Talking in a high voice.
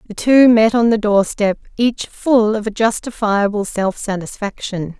Yes: high, 215 Hz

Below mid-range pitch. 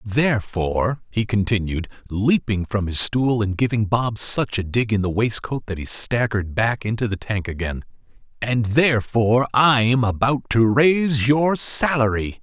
Yes: low, 115 Hz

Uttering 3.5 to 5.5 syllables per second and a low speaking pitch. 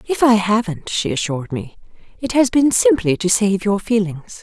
No: 4.9 syllables/s; high, 205 Hz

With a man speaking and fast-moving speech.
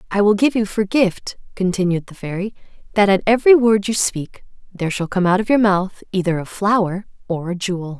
No: female; fast, 210 wpm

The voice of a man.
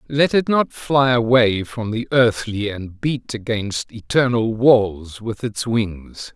Yes: male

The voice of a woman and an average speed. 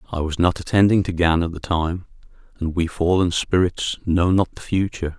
No: male; average, 195 wpm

